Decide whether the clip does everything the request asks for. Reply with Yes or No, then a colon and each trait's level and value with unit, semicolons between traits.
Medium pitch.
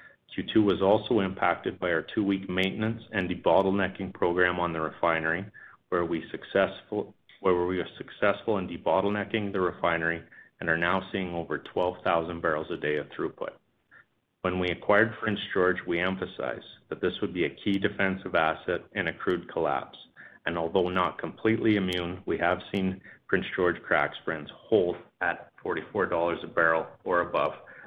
No: very low, 95 Hz